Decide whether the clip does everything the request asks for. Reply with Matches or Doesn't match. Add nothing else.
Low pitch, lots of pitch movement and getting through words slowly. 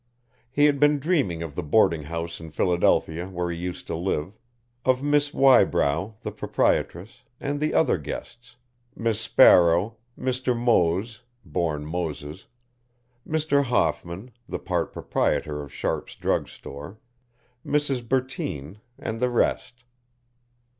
Matches